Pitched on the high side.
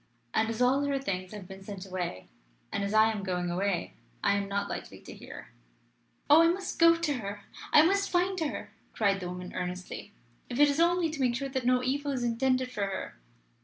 Yes: high, 230 Hz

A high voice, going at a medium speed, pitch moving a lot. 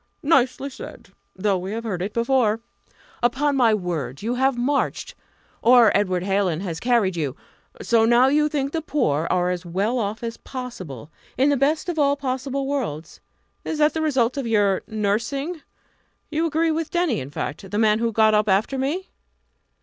Yes: high, 235 Hz; average, 180 wpm; wide, 5.8 semitones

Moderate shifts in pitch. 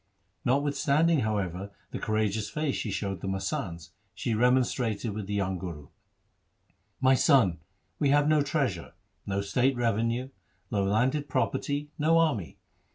No: wide, 6.1 semitones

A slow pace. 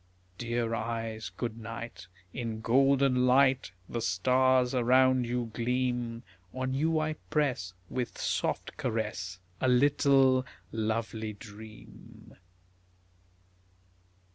Yes: slow, 95 wpm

